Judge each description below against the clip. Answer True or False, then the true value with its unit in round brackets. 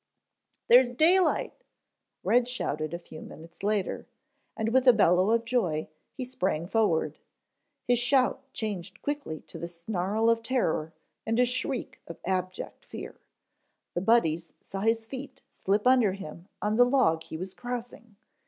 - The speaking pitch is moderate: False (220 Hz)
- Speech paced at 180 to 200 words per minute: False (155 wpm)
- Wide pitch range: True (5.9 semitones)